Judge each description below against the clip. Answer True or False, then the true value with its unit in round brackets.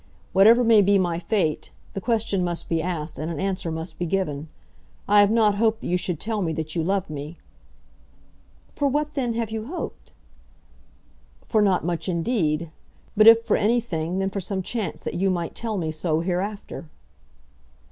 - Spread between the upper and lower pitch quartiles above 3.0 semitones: True (4.7 semitones)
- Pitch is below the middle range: False (190 Hz)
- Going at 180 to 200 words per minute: True (185 wpm)